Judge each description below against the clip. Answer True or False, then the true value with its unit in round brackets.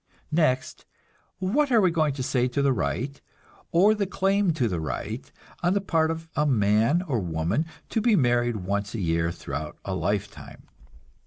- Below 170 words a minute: False (175 wpm)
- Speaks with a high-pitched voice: False (140 Hz)